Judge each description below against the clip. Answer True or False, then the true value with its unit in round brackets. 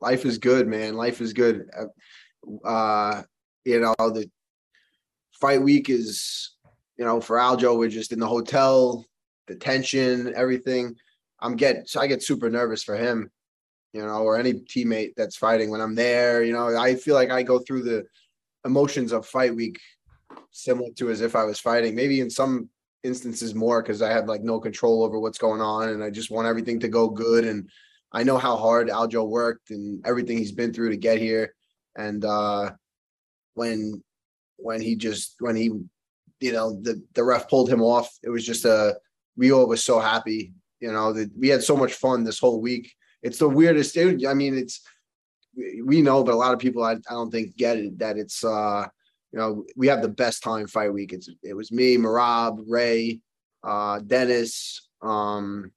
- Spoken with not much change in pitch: True (2.1 semitones)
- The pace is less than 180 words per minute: False (195 wpm)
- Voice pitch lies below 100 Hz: False (115 Hz)